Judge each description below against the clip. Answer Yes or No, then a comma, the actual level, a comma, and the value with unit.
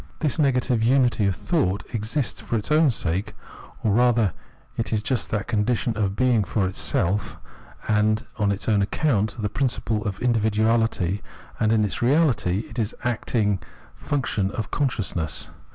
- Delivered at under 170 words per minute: Yes, average, 155 wpm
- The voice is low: Yes, low, 110 Hz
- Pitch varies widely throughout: No, average, 3.2 semitones